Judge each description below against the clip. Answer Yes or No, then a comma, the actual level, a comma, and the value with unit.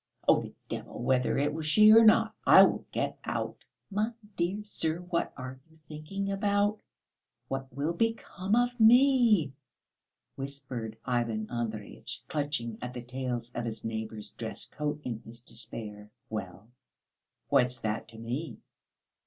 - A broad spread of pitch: Yes, wide, 8.8 semitones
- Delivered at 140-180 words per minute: Yes, average, 145 wpm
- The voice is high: No, low, 135 Hz